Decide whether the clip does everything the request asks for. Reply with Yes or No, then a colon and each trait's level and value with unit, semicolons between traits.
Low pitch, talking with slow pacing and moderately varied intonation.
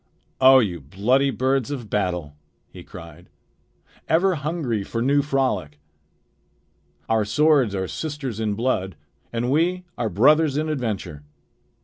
No: low, 125 Hz; slow, 125 wpm; wide, 6.5 semitones